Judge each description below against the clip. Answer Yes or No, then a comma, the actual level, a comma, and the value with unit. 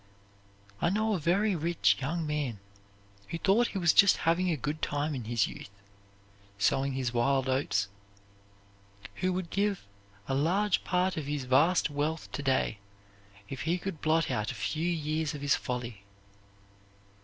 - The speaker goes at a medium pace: Yes, average, 160 wpm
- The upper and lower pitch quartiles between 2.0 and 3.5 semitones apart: No, average, 4.8 semitones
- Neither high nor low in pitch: Yes, medium, 155 Hz